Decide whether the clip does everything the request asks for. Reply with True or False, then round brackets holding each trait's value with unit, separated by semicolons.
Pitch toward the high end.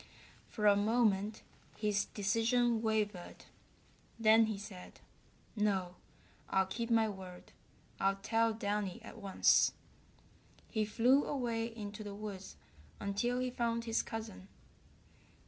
True (215 Hz)